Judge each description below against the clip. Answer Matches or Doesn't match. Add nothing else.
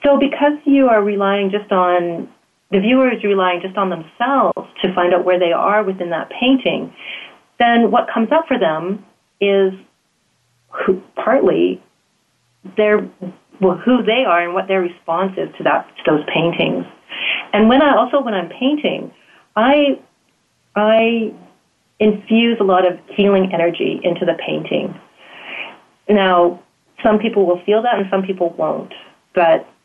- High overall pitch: Matches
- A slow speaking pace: Doesn't match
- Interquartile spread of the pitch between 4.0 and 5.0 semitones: Matches